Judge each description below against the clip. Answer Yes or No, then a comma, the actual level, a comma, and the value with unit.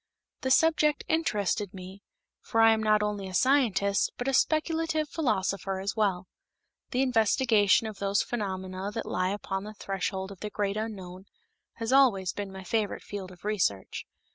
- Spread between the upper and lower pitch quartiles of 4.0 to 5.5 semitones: No, average, 3.3 semitones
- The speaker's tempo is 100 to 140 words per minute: No, average, 165 wpm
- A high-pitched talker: Yes, high, 205 Hz